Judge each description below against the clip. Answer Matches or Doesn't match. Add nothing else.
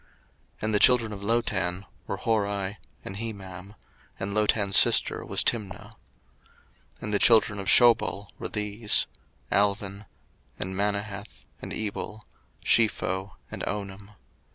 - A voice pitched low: Matches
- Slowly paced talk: Matches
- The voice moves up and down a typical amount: Doesn't match